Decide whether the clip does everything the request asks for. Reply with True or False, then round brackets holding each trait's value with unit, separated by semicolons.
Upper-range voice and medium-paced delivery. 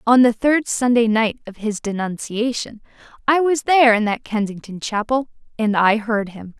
True (230 Hz; 175 wpm)